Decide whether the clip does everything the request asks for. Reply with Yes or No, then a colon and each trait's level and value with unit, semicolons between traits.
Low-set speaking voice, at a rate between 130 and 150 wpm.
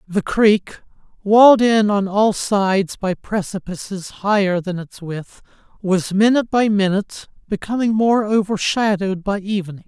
No: high, 200 Hz; slow, 135 wpm